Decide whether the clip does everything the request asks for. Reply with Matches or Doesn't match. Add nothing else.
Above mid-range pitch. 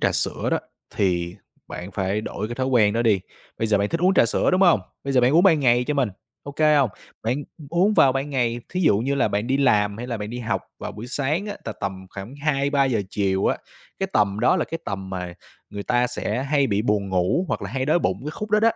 Doesn't match